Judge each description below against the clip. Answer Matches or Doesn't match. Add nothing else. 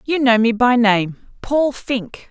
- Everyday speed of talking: Matches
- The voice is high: Matches